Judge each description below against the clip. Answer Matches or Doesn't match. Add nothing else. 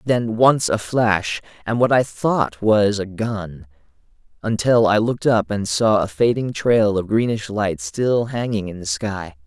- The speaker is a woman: Doesn't match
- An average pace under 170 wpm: Doesn't match